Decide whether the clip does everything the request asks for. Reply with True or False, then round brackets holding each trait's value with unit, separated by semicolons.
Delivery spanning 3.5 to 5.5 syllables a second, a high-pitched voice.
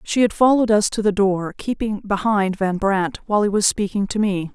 True (5.4 syllables/s; 205 Hz)